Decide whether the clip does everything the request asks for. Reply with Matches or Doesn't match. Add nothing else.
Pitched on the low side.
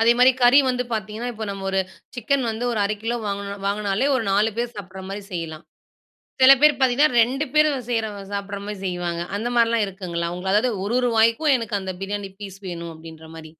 Doesn't match